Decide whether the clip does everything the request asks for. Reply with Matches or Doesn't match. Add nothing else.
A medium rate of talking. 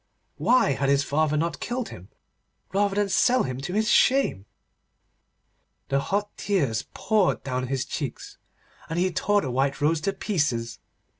Matches